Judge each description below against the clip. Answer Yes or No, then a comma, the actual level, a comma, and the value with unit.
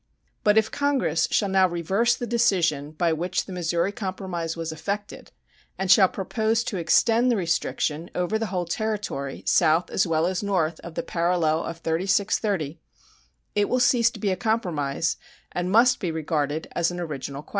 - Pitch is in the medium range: Yes, medium, 180 Hz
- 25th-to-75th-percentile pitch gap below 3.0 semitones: No, average, 4.2 semitones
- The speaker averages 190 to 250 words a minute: No, average, 175 wpm